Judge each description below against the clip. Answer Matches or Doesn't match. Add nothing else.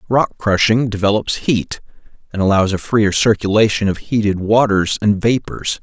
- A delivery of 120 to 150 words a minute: Matches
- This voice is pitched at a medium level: Doesn't match